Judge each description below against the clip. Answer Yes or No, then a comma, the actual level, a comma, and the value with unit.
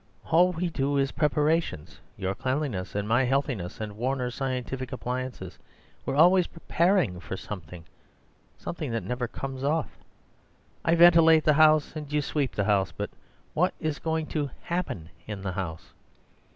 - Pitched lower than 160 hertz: Yes, low, 135 Hz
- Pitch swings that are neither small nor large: No, wide, 6.8 semitones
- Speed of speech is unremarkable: Yes, average, 145 wpm